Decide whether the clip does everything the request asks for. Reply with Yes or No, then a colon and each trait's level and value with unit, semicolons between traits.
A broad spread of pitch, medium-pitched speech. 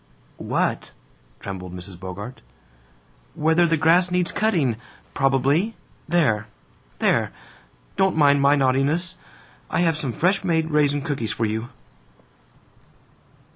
Yes: wide, 5.9 semitones; medium, 145 Hz